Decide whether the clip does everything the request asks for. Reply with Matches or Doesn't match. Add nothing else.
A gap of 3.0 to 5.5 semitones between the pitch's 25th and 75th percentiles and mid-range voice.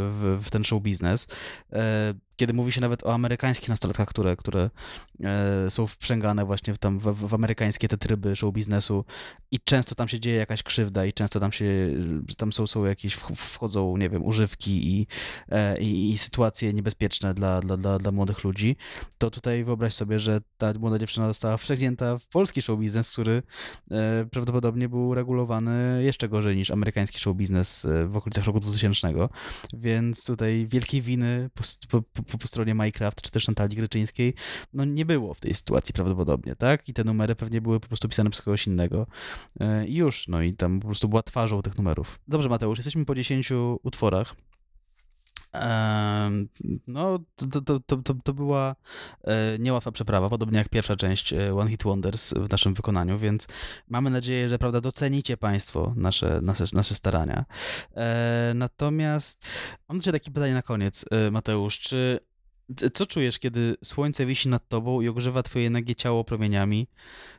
Doesn't match